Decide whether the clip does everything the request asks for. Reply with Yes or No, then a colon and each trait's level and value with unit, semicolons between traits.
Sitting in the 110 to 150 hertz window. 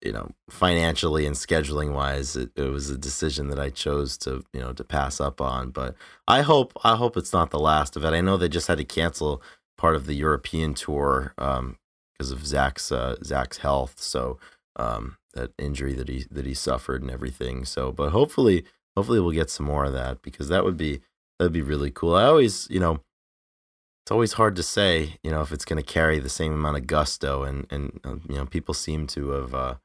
No: very low, 70 Hz